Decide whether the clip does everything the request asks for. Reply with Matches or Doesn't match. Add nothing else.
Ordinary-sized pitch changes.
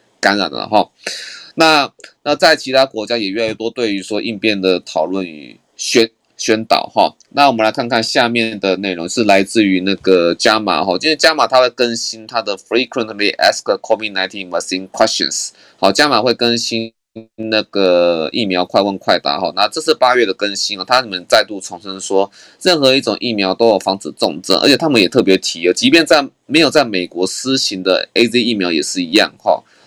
Matches